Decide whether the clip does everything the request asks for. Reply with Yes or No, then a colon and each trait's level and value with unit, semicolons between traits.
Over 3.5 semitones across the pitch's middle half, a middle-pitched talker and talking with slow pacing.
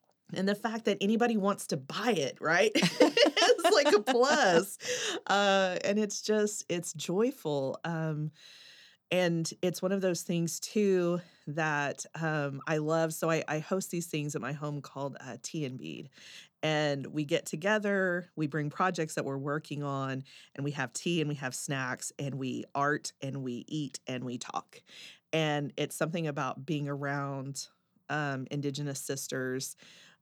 No: average, 4.6 semitones; medium, 155 Hz; average, 165 wpm